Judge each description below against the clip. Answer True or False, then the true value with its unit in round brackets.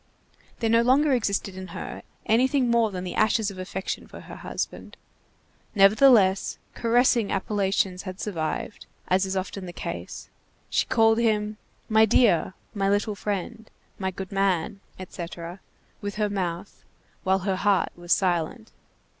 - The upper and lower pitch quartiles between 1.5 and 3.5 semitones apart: True (2.9 semitones)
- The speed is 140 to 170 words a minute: True (145 wpm)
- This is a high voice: True (200 Hz)